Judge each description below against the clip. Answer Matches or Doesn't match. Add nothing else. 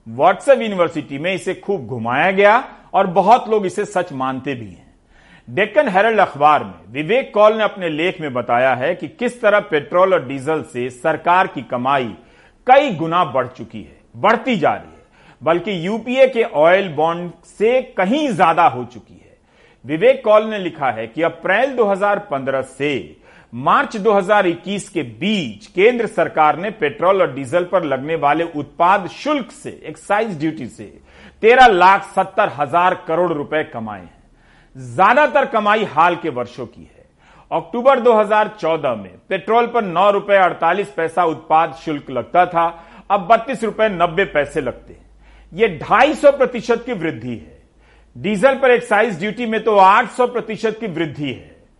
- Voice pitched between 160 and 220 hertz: Matches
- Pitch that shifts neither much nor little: Doesn't match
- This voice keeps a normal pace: Matches